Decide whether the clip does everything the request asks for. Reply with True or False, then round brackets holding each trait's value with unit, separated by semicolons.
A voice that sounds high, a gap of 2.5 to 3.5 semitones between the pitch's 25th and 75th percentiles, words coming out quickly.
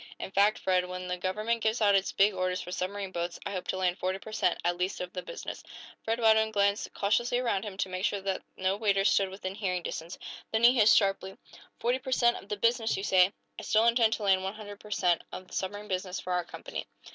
True (195 Hz; 2.9 semitones; 245 wpm)